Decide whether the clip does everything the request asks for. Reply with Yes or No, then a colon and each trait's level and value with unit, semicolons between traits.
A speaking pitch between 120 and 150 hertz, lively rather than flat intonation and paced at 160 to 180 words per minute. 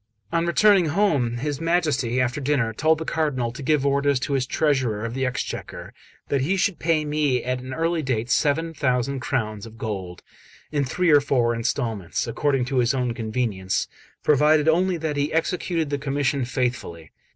No: medium, 140 Hz; average, 4.1 semitones; average, 175 wpm